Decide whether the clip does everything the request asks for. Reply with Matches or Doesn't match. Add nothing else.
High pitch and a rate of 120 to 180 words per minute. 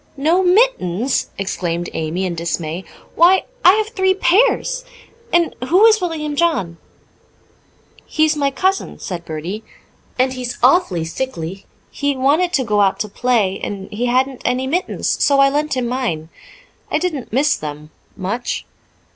Matches